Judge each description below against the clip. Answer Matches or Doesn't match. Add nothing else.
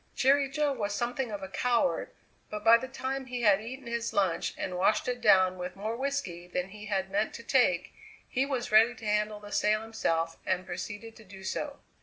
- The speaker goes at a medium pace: Doesn't match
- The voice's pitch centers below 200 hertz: Doesn't match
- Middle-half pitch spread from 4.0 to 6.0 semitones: Matches